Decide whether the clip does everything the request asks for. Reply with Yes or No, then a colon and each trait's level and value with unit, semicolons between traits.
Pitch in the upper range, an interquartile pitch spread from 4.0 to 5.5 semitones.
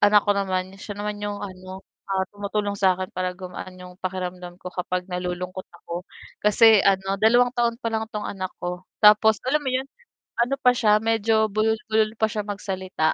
No: high, 200 Hz; average, 2.9 semitones